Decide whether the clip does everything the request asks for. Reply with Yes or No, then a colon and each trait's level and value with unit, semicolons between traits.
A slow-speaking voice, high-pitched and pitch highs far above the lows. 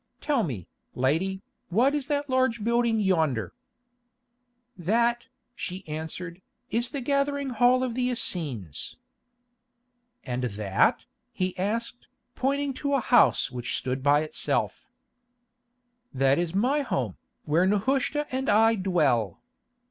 Yes: slow, 120 wpm; high, 205 Hz; wide, 9.0 semitones